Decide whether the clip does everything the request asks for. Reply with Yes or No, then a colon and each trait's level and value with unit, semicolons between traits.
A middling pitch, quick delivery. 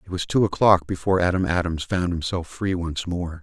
No: very low, 90 Hz; fast, 210 wpm